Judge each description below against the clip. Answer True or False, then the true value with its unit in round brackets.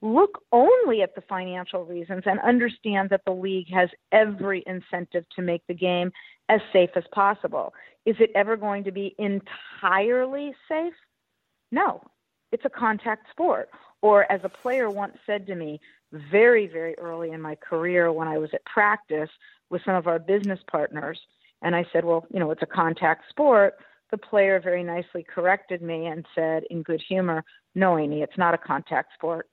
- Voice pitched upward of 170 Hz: True (190 Hz)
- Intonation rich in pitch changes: False (3.7 semitones)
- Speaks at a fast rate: False (180 wpm)